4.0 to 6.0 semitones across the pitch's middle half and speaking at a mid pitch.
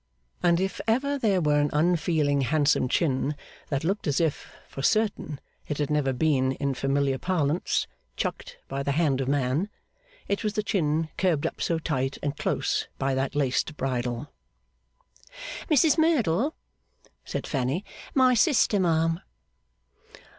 Yes: average, 5.3 semitones; medium, 155 Hz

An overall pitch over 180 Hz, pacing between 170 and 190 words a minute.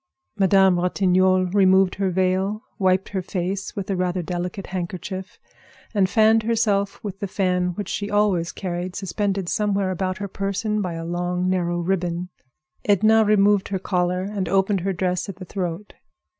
No: high, 190 Hz; average, 160 wpm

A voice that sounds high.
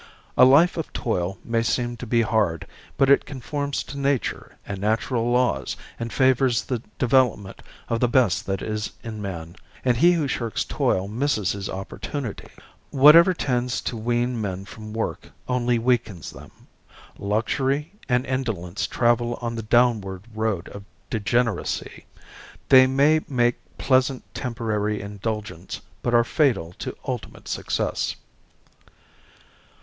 No: low, 120 Hz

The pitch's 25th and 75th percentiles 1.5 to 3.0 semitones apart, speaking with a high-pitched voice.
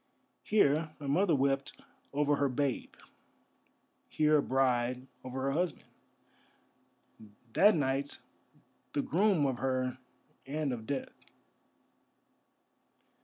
No: average, 2.7 semitones; medium, 140 Hz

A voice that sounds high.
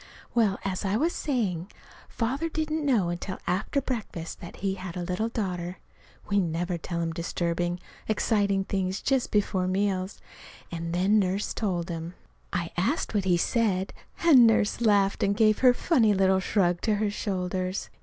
Yes: high, 195 Hz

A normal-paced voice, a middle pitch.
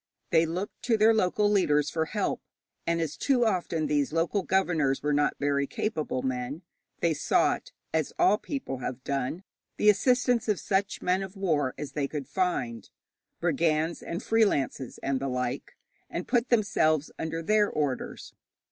Yes: average, 160 wpm; medium, 165 Hz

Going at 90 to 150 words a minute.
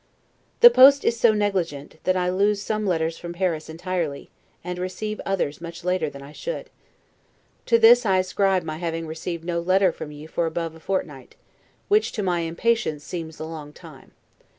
No: average, 180 wpm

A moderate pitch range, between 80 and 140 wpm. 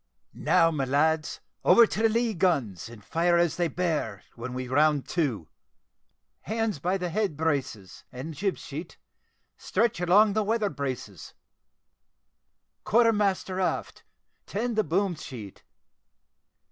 No: wide, 6.8 semitones; slow, 135 wpm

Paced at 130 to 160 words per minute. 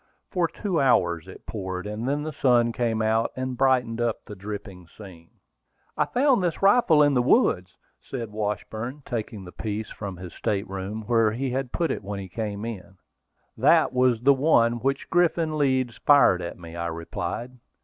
No: average, 185 wpm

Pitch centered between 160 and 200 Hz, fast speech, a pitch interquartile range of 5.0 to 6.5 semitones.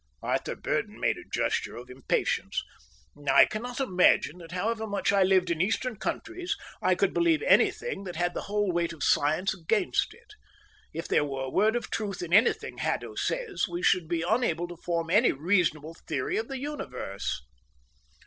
No: medium, 185 Hz; average, 175 wpm; average, 5.3 semitones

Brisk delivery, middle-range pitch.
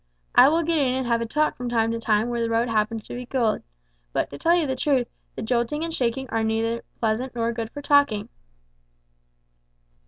No: fast, 215 wpm; high, 235 Hz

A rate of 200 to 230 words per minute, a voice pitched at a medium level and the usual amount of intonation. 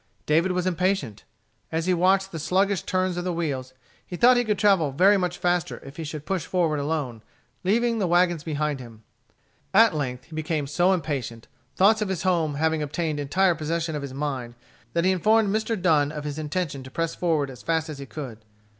Yes: fast, 205 wpm; medium, 165 Hz; average, 4.1 semitones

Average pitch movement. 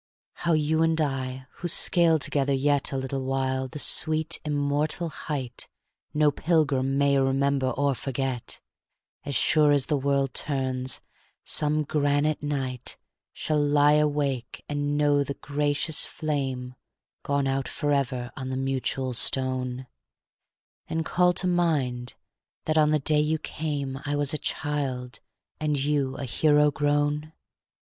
No: narrow, 2.1 semitones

